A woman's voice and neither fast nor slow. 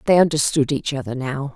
Yes: female; average, 195 wpm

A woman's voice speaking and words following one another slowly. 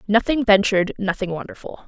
Yes: female; slow, 130 wpm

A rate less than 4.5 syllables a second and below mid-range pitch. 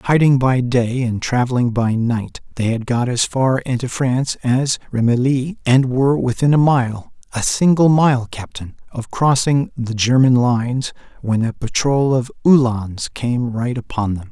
Yes: 4.3 syllables/s; low, 125 Hz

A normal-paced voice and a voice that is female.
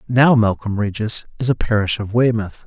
No: average, 180 wpm; male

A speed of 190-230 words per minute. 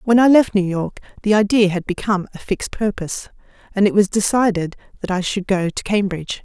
Yes: fast, 205 wpm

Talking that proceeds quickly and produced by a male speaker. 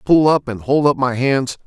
Yes: fast, 250 wpm; male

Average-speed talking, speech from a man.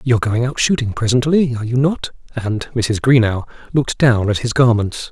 Yes: average, 190 wpm; male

